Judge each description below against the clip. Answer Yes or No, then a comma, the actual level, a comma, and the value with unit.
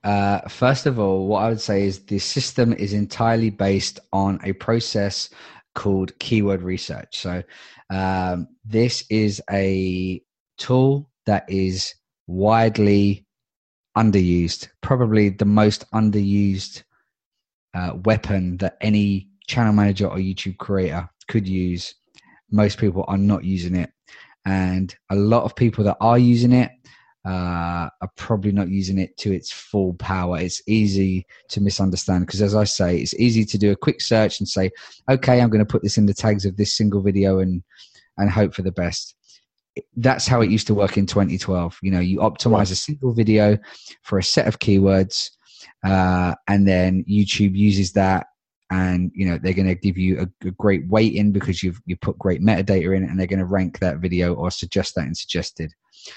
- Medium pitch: No, low, 100 Hz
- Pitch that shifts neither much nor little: No, narrow, 2.3 semitones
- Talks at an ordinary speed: Yes, average, 175 wpm